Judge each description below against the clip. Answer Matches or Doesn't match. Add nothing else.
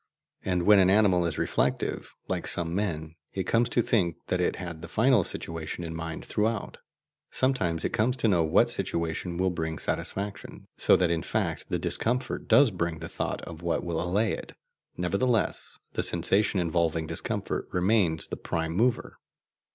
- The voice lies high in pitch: Doesn't match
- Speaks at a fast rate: Doesn't match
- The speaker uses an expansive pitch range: Doesn't match